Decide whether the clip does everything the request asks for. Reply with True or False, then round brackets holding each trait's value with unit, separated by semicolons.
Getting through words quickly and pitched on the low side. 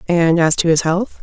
False (245 wpm; 170 Hz)